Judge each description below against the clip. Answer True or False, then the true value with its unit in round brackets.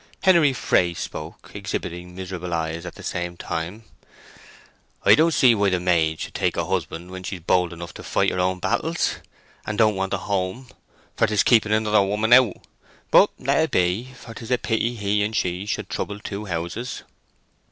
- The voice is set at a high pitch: False (95 Hz)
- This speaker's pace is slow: False (185 wpm)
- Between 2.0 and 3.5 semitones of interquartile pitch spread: False (3.9 semitones)